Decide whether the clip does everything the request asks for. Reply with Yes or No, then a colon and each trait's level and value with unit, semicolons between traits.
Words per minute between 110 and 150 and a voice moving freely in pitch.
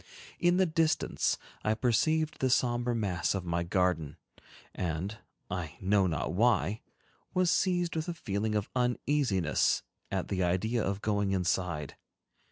Yes: average, 140 wpm; wide, 5.8 semitones